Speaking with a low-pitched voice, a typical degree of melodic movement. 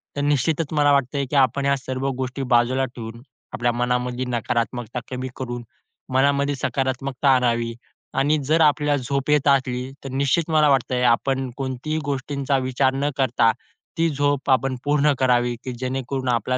No: low, 130 Hz; narrow, 2.3 semitones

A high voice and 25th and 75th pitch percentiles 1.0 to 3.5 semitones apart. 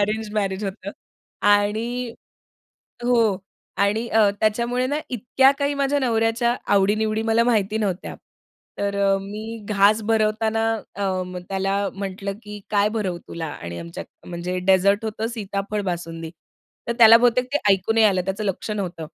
Yes: high, 210 Hz; narrow, 2.5 semitones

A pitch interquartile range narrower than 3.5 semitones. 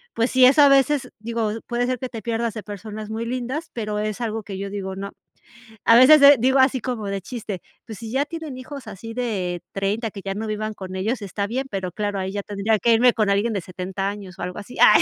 No: average, 3.8 semitones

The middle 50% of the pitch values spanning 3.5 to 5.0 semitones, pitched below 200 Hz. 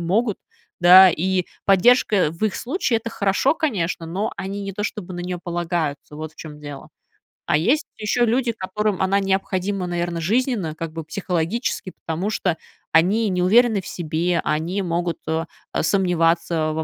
Yes: average, 3.8 semitones; medium, 185 Hz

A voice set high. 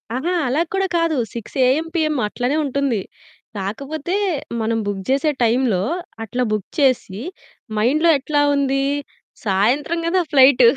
Yes: very high, 270 Hz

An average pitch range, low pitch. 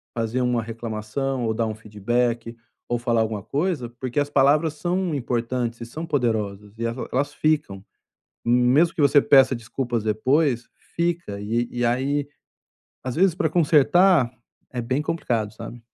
Yes: average, 4.0 semitones; low, 125 Hz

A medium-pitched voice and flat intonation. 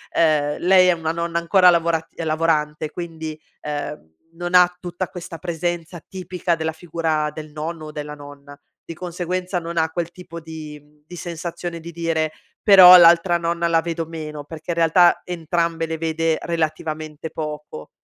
Yes: medium, 165 Hz; narrow, 1.8 semitones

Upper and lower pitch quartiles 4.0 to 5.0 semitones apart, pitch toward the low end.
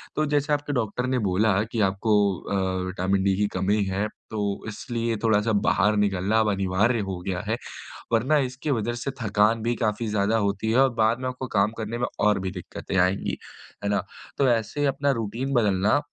No: average, 3.3 semitones; low, 110 Hz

